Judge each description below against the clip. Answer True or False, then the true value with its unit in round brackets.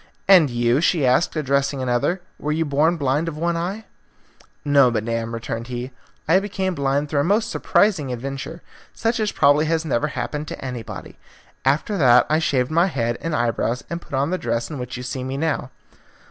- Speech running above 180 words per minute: True (190 wpm)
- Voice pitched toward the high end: False (145 Hz)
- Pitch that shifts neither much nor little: True (4.8 semitones)